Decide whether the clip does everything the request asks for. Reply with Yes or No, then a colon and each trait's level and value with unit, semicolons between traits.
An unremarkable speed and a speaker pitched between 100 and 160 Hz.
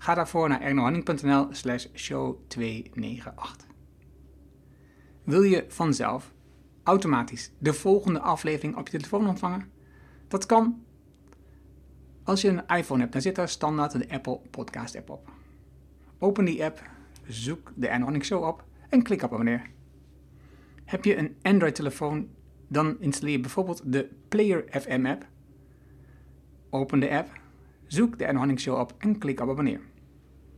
No: slow, 130 wpm; low, 135 Hz